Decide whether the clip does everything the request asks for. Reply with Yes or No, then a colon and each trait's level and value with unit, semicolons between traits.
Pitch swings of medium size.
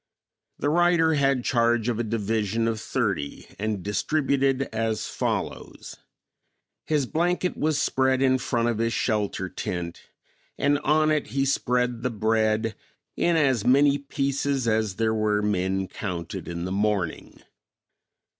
Yes: average, 4.6 semitones